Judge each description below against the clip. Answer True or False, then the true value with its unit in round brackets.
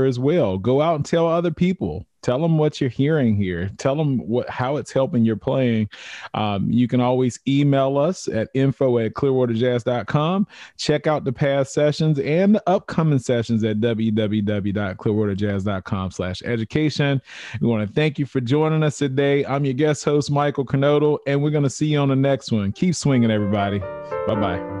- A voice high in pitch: False (135 Hz)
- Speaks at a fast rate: False (175 wpm)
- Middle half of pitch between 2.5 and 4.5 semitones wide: False (5.0 semitones)